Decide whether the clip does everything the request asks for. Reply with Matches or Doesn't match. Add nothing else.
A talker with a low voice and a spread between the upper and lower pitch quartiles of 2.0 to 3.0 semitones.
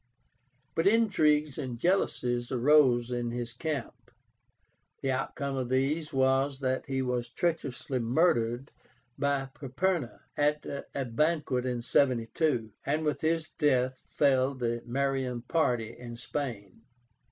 Doesn't match